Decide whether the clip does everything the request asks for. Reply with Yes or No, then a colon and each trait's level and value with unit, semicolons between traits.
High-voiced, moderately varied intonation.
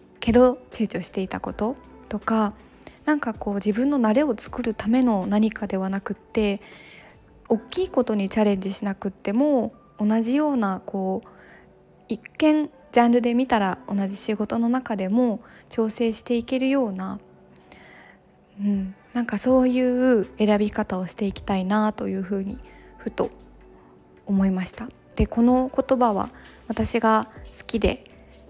Yes: high, 215 Hz; average, 3.5 semitones